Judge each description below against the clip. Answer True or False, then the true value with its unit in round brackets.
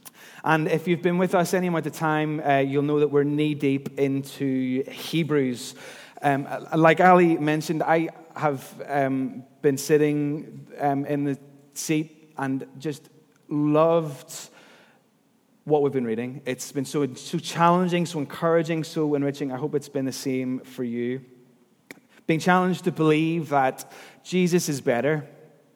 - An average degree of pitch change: True (3.0 semitones)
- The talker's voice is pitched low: False (150 Hz)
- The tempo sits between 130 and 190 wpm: True (150 wpm)